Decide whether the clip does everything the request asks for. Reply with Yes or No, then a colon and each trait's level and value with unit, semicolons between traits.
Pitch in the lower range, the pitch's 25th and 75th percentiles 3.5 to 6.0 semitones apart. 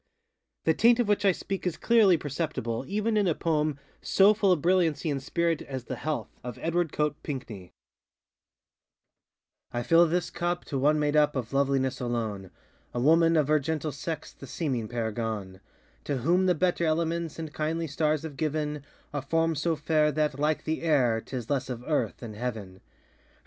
No: medium, 150 Hz; average, 4.2 semitones